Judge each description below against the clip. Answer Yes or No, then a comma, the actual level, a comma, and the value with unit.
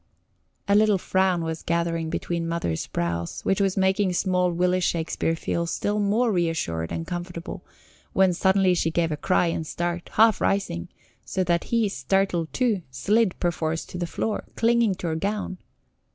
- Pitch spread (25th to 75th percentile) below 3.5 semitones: Yes, average, 2.8 semitones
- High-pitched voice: No, medium, 180 Hz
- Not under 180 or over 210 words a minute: No, average, 165 wpm